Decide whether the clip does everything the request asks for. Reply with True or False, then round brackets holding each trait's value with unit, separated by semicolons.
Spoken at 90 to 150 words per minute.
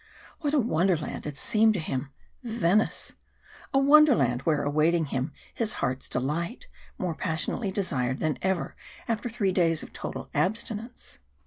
True (145 wpm)